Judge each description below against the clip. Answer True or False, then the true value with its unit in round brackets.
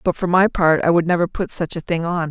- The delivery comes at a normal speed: False (315 wpm)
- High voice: False (170 Hz)